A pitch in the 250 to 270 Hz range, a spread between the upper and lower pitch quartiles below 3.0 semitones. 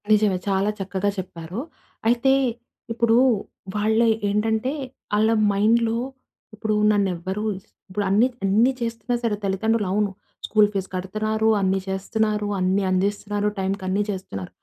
No: high, 205 Hz; narrow, 2.4 semitones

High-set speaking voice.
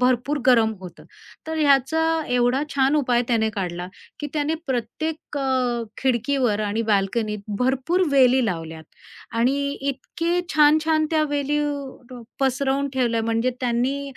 Yes: very high, 255 Hz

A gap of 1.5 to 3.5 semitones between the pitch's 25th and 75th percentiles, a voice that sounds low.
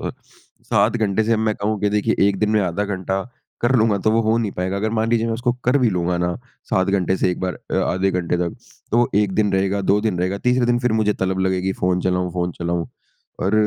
Yes: average, 3.0 semitones; low, 100 Hz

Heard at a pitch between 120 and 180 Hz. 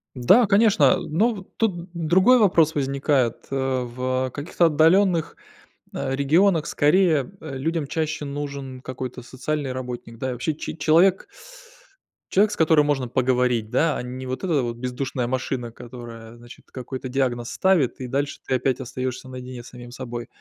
Yes: low, 135 Hz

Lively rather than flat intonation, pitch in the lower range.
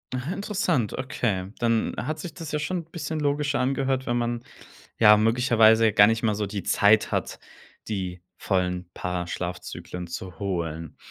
Yes: wide, 6.5 semitones; low, 115 Hz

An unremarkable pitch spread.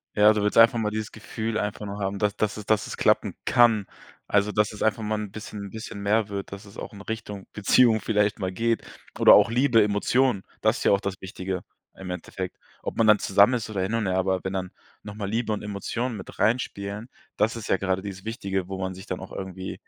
No: narrow, 2.1 semitones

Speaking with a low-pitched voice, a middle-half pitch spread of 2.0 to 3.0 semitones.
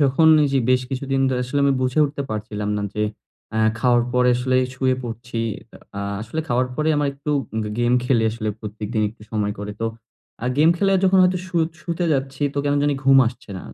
No: low, 130 Hz; average, 4.0 semitones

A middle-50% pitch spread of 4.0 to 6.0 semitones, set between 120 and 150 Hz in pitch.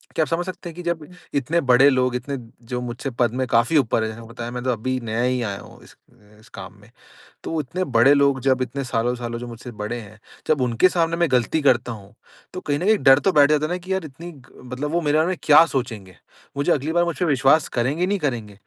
Yes: average, 4.8 semitones; low, 135 Hz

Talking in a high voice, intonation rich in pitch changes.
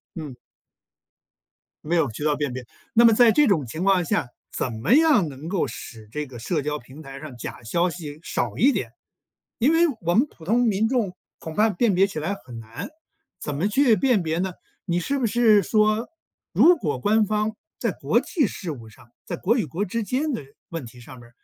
No: medium, 180 Hz; wide, 7.4 semitones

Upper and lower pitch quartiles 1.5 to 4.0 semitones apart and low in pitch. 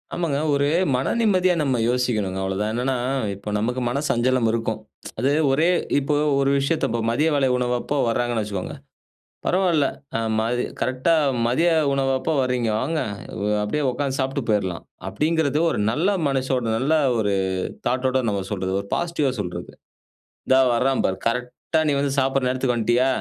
Yes: average, 3.4 semitones; low, 130 Hz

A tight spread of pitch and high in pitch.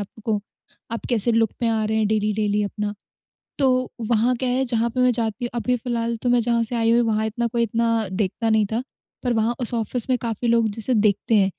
Yes: narrow, 1.7 semitones; high, 230 Hz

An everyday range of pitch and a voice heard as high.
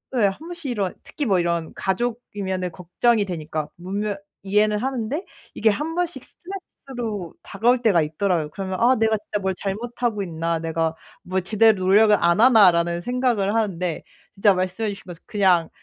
Yes: average, 4.2 semitones; high, 200 Hz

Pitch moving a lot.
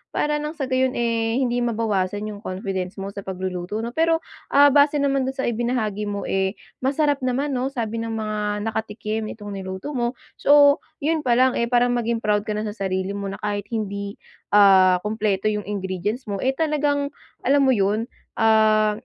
No: average, 4.4 semitones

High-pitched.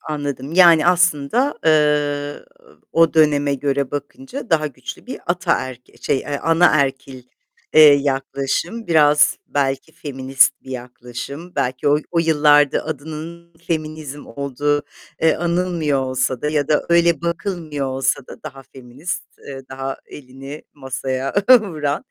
No: medium, 145 Hz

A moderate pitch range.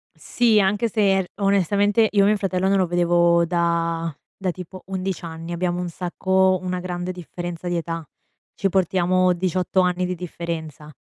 No: narrow, 1.9 semitones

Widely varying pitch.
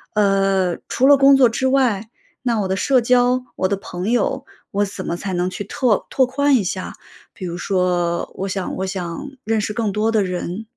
No: average, 4.8 semitones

